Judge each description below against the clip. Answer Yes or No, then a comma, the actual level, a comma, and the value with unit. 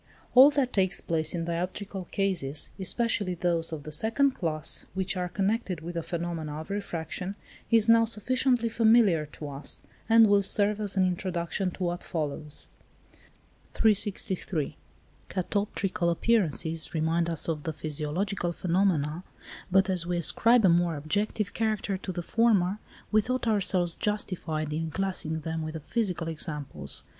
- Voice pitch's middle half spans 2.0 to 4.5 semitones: Yes, average, 4.1 semitones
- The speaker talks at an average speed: Yes, average, 150 wpm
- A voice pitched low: No, medium, 180 Hz